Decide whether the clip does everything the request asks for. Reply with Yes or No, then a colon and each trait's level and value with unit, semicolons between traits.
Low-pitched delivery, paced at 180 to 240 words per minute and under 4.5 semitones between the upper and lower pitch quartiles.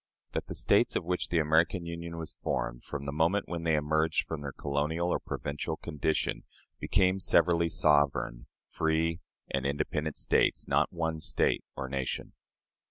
No: very low, 80 Hz; average, 160 wpm; narrow, 2.5 semitones